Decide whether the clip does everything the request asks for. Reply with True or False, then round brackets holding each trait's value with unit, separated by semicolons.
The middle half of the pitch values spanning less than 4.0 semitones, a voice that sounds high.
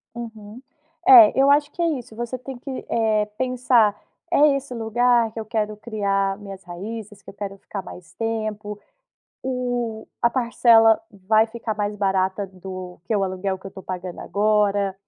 True (3.3 semitones; 215 Hz)